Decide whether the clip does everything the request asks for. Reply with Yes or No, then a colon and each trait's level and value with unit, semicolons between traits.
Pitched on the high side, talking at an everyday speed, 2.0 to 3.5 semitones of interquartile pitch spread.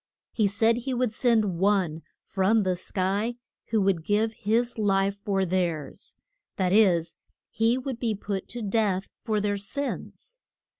Yes: high, 205 Hz; average, 150 wpm; average, 3.0 semitones